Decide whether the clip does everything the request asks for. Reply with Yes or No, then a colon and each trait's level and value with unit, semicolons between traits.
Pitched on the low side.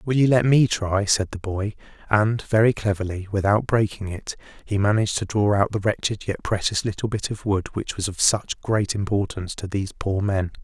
Yes: low, 105 Hz